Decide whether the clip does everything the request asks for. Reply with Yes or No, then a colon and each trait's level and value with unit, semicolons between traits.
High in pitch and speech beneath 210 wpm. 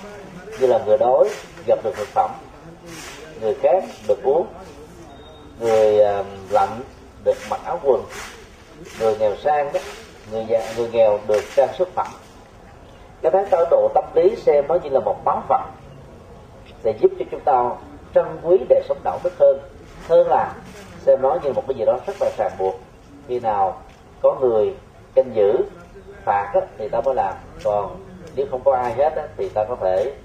Yes: high, 215 Hz; average, 185 wpm